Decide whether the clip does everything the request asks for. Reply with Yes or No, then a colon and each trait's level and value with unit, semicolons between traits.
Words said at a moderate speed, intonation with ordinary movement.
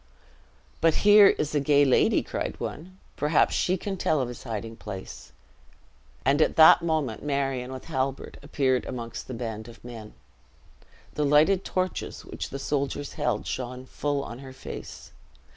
Yes: average, 155 wpm; average, 3.7 semitones